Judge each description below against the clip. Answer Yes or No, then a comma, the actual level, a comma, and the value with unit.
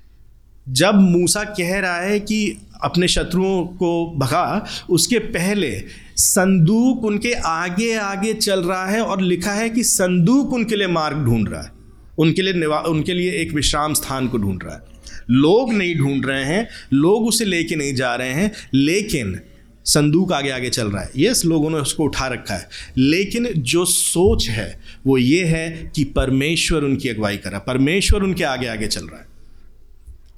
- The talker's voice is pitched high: No, medium, 160 Hz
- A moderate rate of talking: Yes, average, 170 wpm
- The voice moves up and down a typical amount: No, wide, 6.6 semitones